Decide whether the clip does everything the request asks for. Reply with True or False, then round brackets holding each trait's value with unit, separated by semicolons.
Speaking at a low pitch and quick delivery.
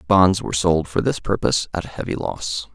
True (85 Hz; 220 wpm)